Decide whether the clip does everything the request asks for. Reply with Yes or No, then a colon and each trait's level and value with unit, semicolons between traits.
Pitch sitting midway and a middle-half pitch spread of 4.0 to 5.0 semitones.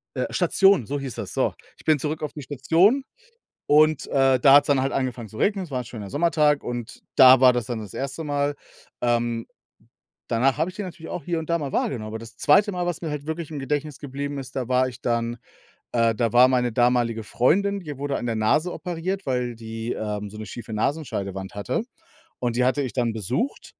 No: low, 130 Hz; average, 4.5 semitones